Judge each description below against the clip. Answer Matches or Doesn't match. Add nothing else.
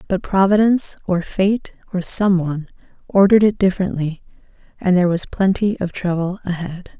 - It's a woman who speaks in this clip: Matches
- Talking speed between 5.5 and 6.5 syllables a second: Matches